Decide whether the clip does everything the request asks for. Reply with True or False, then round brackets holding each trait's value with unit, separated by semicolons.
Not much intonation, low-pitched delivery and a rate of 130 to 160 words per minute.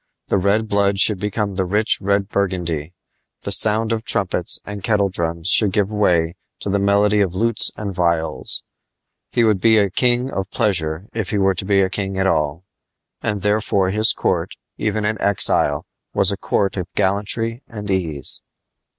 False (2.1 semitones; 100 Hz; 170 wpm)